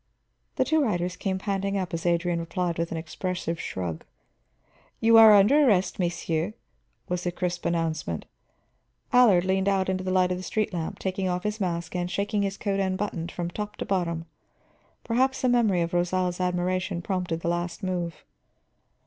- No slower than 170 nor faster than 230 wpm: Yes, average, 175 wpm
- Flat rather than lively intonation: Yes, narrow, 2.3 semitones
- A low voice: No, medium, 185 Hz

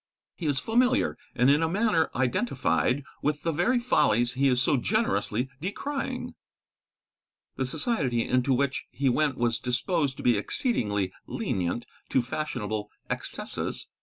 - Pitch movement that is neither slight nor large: No, wide, 6.3 semitones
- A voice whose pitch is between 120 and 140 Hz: Yes, low, 135 Hz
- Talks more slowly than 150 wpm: Yes, slow, 135 wpm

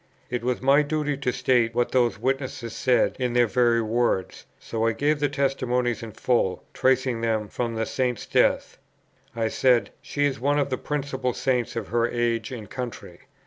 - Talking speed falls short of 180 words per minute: No, average, 185 wpm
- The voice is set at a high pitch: No, low, 125 Hz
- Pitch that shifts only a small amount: Yes, narrow, 2.3 semitones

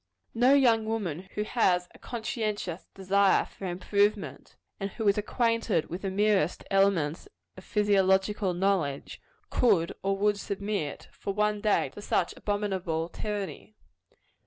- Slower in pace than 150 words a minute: Yes, slow, 135 wpm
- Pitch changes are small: Yes, narrow, 2.1 semitones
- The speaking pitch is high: Yes, high, 200 Hz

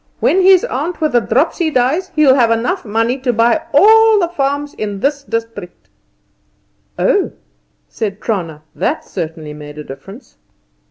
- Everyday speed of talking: Yes, average, 150 wpm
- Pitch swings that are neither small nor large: No, wide, 7.2 semitones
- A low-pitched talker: No, high, 245 Hz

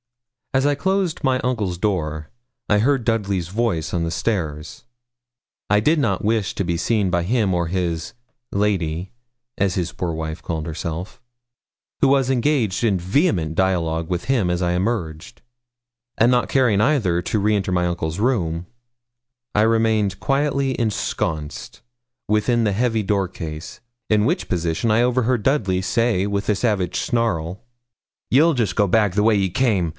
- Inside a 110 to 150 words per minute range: No, average, 160 wpm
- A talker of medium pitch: No, low, 100 Hz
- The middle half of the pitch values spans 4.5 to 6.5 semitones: Yes, average, 5.0 semitones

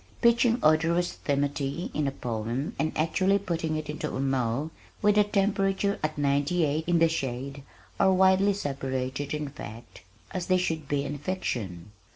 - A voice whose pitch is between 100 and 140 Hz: No, medium, 155 Hz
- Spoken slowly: No, average, 165 wpm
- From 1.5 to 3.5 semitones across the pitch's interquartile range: No, average, 5.1 semitones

